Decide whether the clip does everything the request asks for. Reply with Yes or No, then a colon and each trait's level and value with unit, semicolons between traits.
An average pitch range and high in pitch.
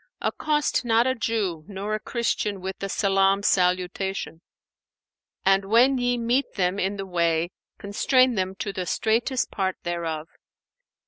Yes: average, 3.8 semitones; high, 195 Hz